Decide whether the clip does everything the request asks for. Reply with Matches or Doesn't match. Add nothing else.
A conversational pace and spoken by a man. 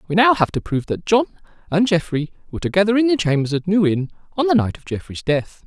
Doesn't match